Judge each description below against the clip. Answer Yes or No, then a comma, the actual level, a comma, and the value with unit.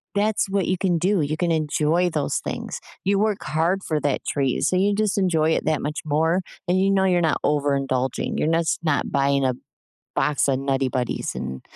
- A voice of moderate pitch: Yes, medium, 160 Hz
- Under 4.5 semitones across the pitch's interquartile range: No, average, 4.9 semitones